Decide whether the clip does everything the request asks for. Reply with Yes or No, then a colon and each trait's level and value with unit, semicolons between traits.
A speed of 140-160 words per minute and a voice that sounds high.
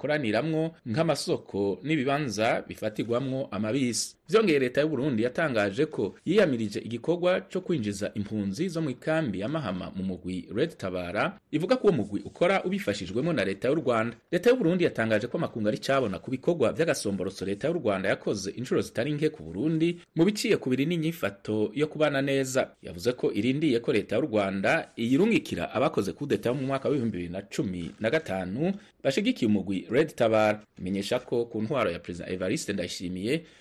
No: average, 155 wpm; low, 120 Hz